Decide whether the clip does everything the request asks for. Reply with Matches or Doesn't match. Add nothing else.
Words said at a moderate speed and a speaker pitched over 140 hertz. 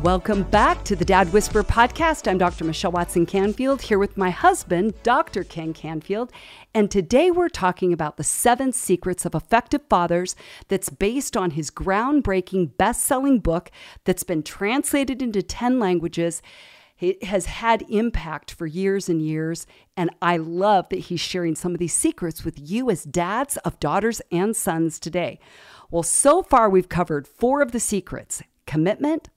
Matches